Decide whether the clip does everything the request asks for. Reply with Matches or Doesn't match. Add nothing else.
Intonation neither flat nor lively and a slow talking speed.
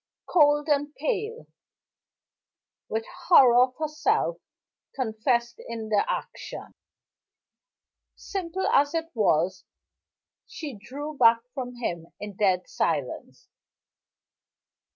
Doesn't match